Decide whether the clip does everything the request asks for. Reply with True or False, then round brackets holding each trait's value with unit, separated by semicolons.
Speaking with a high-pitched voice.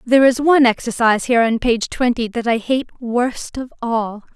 True (240 Hz)